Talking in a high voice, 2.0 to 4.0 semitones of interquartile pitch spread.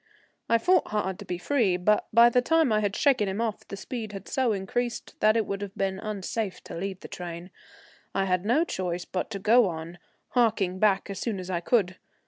Yes: high, 200 Hz; average, 3.7 semitones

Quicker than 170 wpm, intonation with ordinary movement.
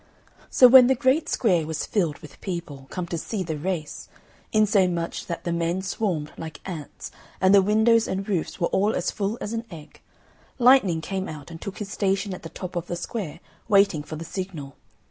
Yes: average, 200 wpm; average, 4.0 semitones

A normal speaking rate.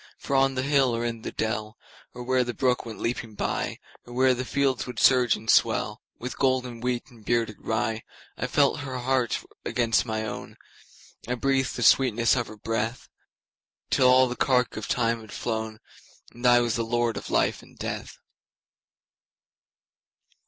Yes: average, 150 wpm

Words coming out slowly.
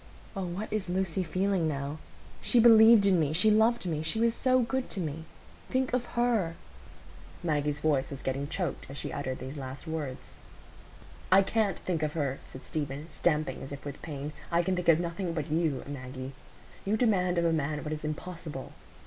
No: average, 185 wpm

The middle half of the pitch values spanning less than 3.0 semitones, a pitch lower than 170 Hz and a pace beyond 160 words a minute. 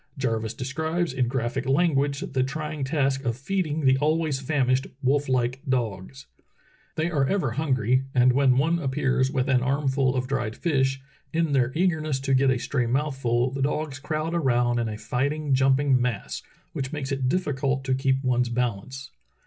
Yes: narrow, 2.5 semitones; low, 135 Hz; average, 170 wpm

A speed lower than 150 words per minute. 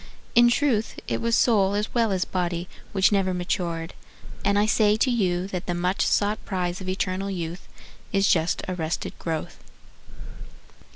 No: average, 160 wpm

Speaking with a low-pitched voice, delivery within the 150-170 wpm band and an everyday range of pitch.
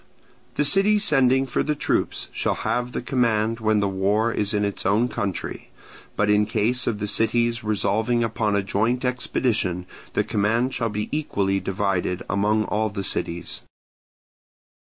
Yes: low, 110 Hz; average, 155 wpm; average, 3.2 semitones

